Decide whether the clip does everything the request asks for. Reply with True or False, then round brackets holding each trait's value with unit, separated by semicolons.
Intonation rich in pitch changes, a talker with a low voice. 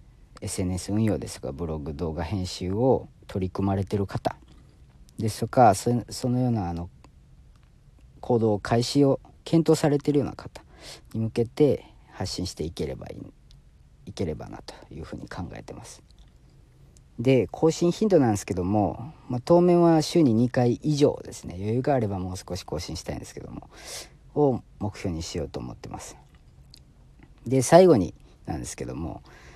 True (6.1 semitones; 110 Hz)